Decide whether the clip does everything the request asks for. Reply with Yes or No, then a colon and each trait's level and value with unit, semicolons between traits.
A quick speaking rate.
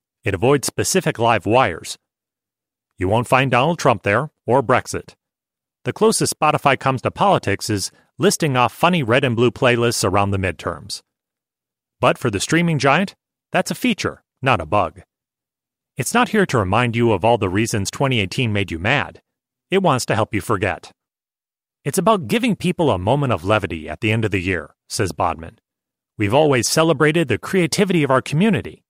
No: average, 175 wpm